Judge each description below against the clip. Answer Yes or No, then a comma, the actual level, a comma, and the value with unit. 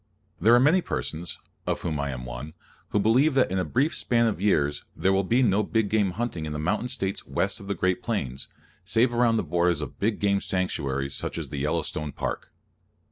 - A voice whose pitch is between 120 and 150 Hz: No, very low, 95 Hz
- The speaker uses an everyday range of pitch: No, wide, 6.9 semitones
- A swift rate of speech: Yes, fast, 215 wpm